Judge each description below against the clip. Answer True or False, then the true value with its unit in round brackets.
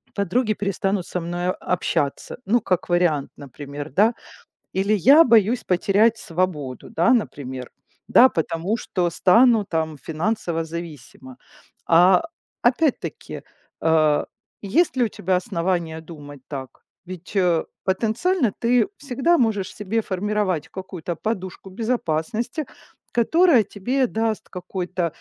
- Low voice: False (185 Hz)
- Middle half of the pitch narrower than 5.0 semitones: False (5.4 semitones)